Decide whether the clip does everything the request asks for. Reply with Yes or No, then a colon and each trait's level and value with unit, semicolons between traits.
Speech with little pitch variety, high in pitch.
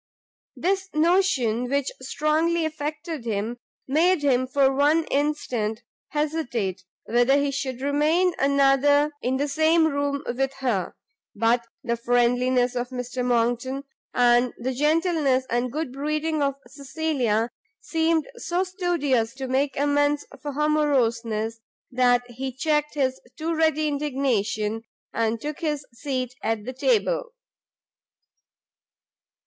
No: average, 3.8 semitones; very high, 275 Hz